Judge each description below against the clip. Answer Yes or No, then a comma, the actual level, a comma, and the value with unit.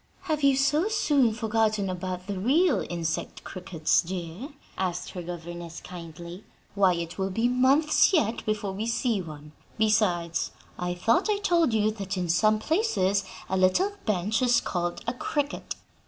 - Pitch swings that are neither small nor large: No, wide, 5.9 semitones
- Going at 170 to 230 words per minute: No, average, 155 wpm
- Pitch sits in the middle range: No, high, 205 Hz